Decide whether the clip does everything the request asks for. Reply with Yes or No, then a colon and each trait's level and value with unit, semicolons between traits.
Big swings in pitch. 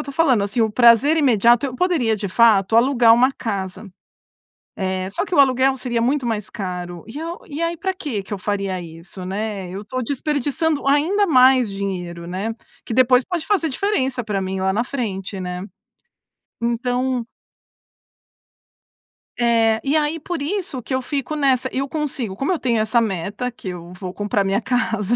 Yes: wide, 5.7 semitones